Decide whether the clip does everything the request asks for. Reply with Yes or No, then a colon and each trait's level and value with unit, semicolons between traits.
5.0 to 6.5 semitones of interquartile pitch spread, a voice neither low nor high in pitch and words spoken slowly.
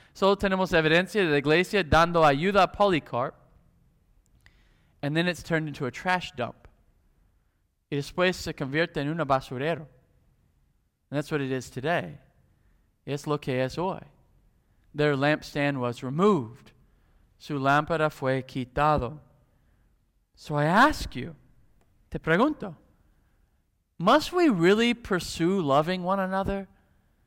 Yes: wide, 5.6 semitones; medium, 150 Hz; slow, 125 wpm